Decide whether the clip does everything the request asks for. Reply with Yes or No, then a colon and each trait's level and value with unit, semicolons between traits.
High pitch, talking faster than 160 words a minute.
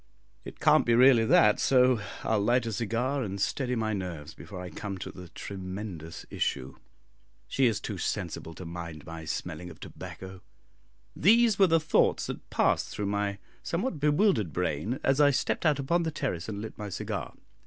No: low, 105 Hz; average, 180 wpm